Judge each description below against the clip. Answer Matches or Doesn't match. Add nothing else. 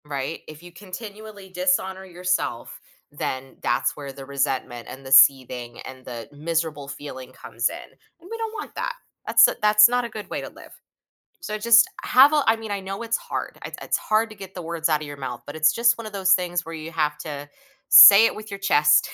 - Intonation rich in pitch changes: Matches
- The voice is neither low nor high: Matches